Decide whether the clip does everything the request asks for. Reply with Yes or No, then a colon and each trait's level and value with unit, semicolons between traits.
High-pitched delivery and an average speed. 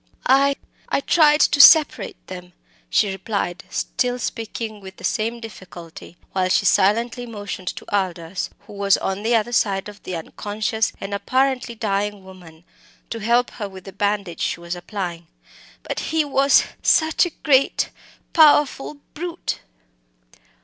Yes: high, 210 Hz; average, 145 wpm